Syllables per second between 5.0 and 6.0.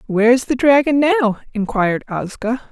Yes: 5.2 syllables/s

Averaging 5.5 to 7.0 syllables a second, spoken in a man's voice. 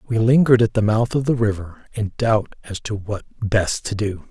No: 5.3 syllables/s; male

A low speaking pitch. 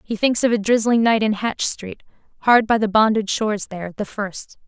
No: high, 215 Hz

